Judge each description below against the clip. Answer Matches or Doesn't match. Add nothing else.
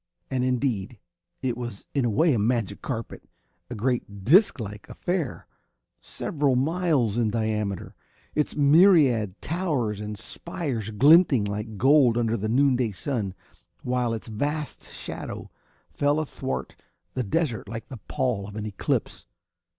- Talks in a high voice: Doesn't match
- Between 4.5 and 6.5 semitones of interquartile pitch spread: Matches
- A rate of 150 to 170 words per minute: Doesn't match